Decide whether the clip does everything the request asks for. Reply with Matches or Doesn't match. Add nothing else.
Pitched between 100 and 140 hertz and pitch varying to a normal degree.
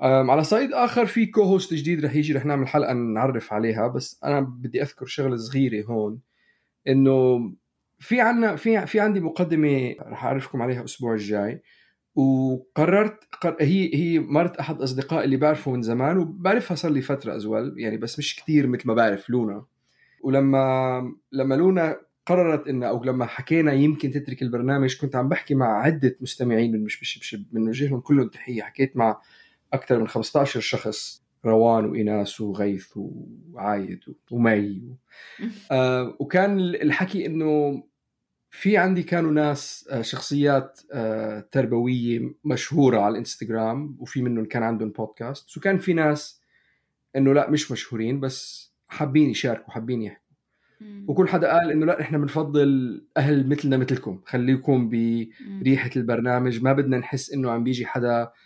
Matches